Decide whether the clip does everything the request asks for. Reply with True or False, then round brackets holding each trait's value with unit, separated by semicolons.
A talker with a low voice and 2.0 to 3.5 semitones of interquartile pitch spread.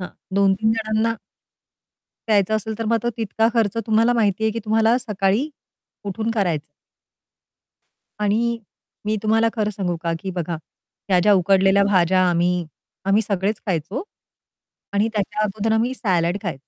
False (210 Hz; 2.8 semitones)